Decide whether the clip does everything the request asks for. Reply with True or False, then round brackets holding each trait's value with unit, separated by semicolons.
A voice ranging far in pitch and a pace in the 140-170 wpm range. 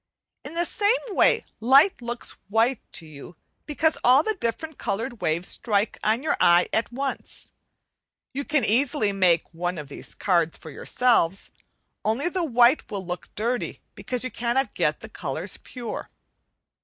True (5.9 semitones; 160 wpm)